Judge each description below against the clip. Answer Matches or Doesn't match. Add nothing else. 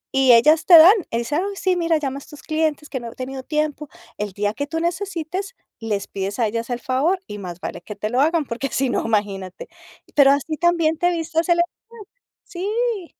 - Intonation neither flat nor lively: Doesn't match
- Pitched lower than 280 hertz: Doesn't match